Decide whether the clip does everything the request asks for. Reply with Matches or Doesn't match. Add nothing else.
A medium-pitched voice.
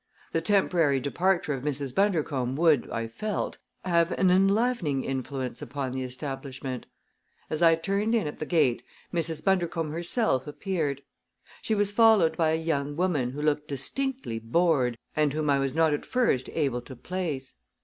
Matches